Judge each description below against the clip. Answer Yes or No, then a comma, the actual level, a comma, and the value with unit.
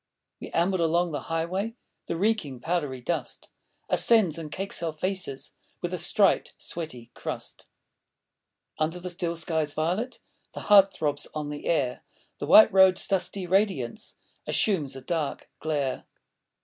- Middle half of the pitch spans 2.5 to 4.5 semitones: Yes, average, 4.0 semitones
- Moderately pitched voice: Yes, medium, 170 Hz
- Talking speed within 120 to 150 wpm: Yes, average, 140 wpm